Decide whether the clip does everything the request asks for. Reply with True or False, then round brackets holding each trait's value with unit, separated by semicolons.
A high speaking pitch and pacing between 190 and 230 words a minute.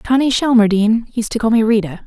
True (225 Hz; 205 wpm)